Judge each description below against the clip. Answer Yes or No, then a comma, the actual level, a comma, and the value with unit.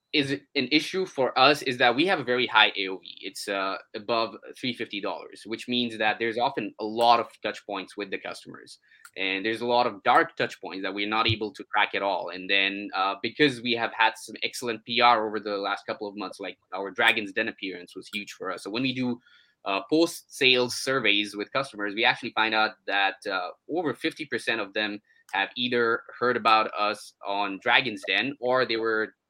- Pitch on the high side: No, low, 115 Hz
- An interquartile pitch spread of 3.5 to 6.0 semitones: No, average, 3.1 semitones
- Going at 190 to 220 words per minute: Yes, fast, 205 wpm